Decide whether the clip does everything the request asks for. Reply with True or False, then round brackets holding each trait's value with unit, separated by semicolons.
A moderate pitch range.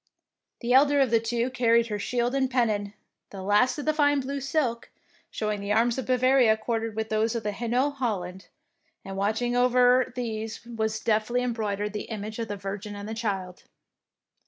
True (3.0 semitones)